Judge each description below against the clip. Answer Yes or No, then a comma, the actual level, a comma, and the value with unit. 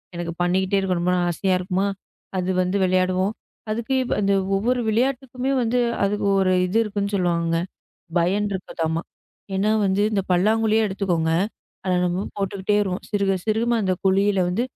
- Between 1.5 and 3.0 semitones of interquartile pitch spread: Yes, narrow, 2.4 semitones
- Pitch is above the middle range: Yes, high, 195 Hz